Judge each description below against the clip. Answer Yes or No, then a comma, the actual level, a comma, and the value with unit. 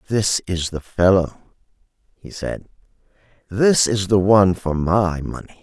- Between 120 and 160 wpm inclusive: Yes, average, 140 wpm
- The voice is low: Yes, very low, 95 Hz